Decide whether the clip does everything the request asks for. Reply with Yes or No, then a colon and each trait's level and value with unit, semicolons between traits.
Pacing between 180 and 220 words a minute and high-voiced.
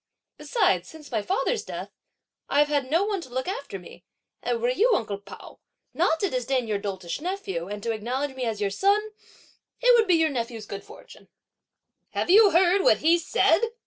Yes: average, 190 wpm; very high, 290 Hz